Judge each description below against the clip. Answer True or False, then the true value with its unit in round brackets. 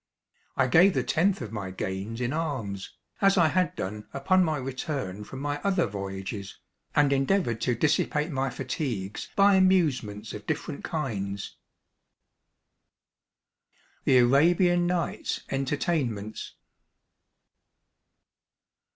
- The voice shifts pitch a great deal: True (7.7 semitones)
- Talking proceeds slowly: True (110 wpm)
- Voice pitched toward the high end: False (135 Hz)